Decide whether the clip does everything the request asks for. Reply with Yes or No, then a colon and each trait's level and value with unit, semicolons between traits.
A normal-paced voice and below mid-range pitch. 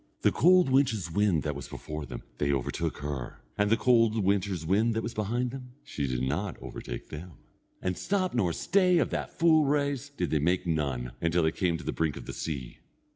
No: fast, 210 wpm; very low, 95 Hz